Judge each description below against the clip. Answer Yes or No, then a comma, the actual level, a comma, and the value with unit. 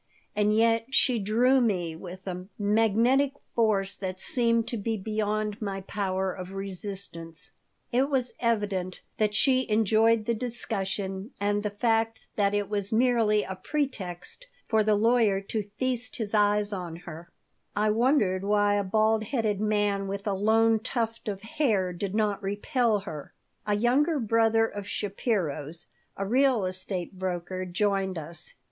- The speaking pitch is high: Yes, high, 210 Hz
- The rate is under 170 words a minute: Yes, average, 150 wpm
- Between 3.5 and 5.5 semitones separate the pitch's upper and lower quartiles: No, average, 2.8 semitones